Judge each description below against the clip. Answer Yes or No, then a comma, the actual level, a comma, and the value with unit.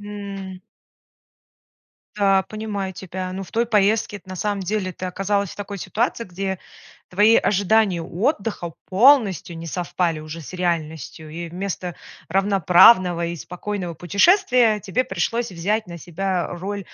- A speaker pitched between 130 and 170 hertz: No, high, 190 Hz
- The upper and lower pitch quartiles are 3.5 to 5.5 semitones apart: No, average, 2.9 semitones